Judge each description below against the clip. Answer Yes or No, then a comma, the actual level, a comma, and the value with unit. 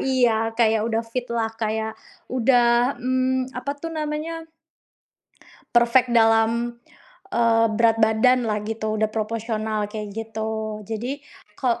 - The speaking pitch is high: Yes, high, 230 Hz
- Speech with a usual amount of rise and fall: No, narrow, 2.2 semitones